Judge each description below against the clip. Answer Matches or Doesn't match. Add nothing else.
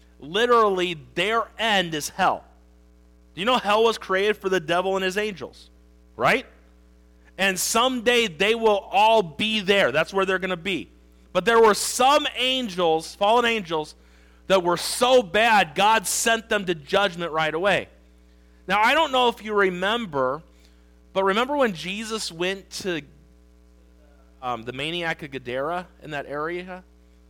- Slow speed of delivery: Doesn't match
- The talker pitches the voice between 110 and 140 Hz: Doesn't match